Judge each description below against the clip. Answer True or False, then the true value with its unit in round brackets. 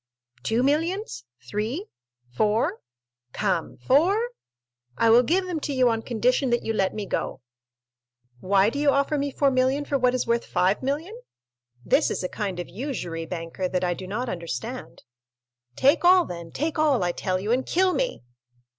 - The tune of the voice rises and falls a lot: True (7.5 semitones)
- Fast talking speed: False (160 wpm)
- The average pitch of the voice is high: True (240 Hz)